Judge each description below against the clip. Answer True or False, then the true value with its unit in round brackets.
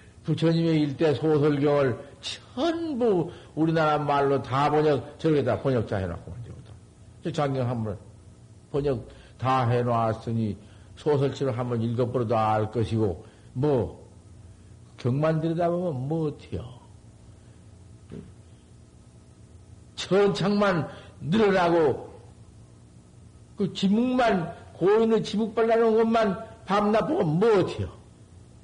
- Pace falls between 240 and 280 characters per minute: False (205 characters per minute)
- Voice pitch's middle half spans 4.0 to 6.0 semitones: False (7.2 semitones)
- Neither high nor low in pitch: False (130 Hz)